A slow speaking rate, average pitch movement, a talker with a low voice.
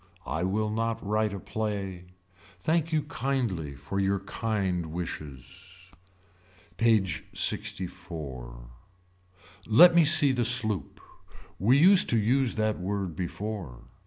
Yes: slow, 115 wpm; average, 4.4 semitones; low, 100 Hz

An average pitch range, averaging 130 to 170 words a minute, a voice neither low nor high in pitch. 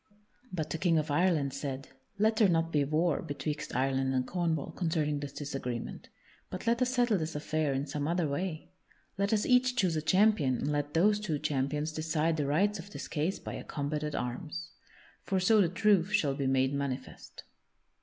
No: average, 4.5 semitones; average, 195 wpm; medium, 155 Hz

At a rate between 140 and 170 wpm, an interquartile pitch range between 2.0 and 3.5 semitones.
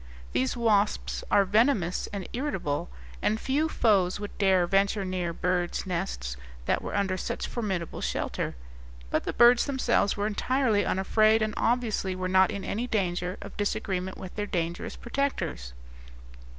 Yes: average, 150 wpm; average, 3.2 semitones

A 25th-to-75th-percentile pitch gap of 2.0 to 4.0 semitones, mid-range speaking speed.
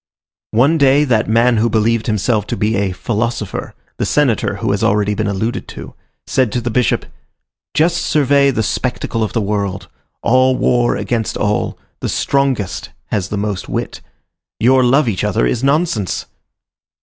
Yes: average, 3.7 semitones; average, 160 wpm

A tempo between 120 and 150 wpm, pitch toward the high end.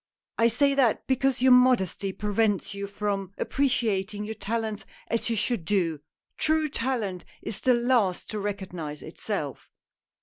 Yes: average, 140 wpm; high, 215 Hz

